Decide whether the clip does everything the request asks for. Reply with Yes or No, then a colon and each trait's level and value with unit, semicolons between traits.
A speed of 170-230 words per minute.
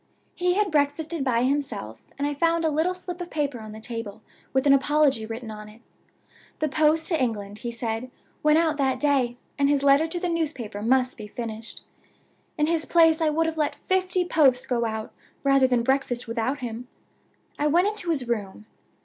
Yes: average, 195 wpm